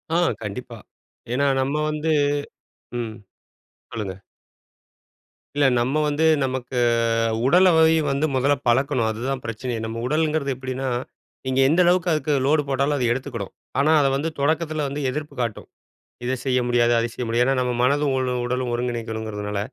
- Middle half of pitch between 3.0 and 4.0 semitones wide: Yes, average, 3.7 semitones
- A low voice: Yes, low, 130 Hz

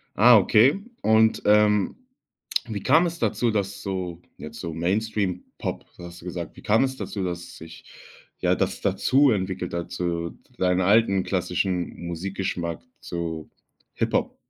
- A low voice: Yes, very low, 95 Hz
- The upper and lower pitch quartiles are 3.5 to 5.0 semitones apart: Yes, average, 3.8 semitones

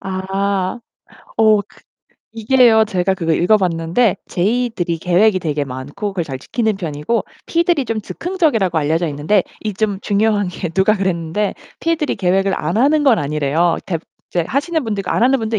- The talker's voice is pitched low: No, high, 195 Hz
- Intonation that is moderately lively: Yes, average, 4.6 semitones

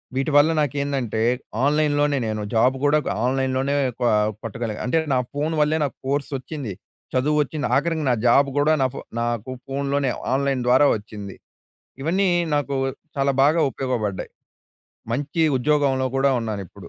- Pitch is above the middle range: No, medium, 140 Hz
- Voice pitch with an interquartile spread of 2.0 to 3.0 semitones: Yes, average, 2.7 semitones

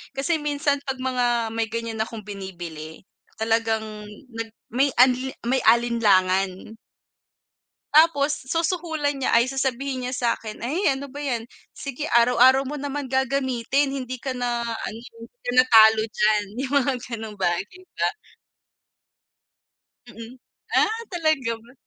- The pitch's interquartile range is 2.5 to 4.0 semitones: Yes, average, 3.6 semitones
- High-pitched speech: Yes, very high, 250 Hz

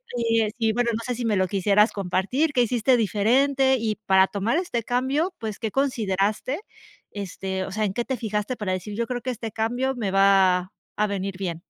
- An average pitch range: Yes, average, 3.9 semitones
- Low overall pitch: No, high, 220 Hz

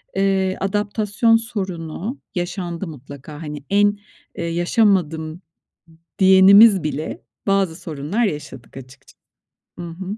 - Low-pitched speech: No, medium, 185 Hz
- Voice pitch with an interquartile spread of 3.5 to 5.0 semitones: Yes, average, 4.1 semitones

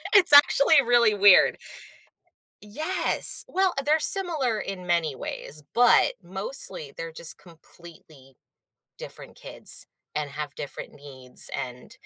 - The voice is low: No, medium, 180 Hz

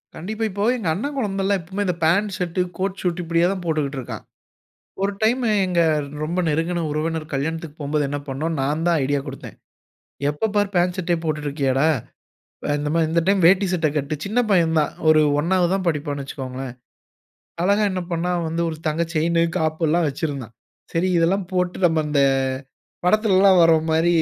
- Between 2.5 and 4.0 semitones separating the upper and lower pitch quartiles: Yes, average, 3.4 semitones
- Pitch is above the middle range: No, medium, 165 Hz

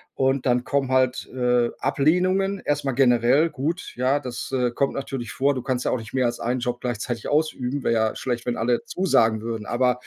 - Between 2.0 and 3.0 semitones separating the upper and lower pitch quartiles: Yes, narrow, 2.4 semitones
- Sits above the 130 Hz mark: No, low, 125 Hz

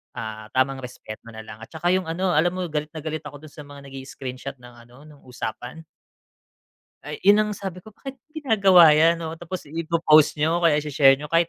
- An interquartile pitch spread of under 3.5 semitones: No, average, 4.3 semitones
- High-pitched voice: No, medium, 155 Hz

